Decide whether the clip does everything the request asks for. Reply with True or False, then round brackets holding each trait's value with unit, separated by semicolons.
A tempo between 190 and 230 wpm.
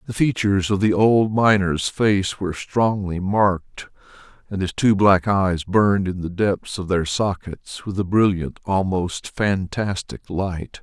False (155 wpm)